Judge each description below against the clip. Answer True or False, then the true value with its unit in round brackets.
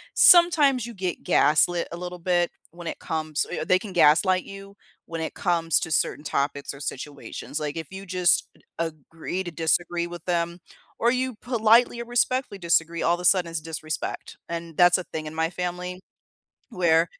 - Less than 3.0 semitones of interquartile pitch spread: True (2.6 semitones)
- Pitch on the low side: False (175 Hz)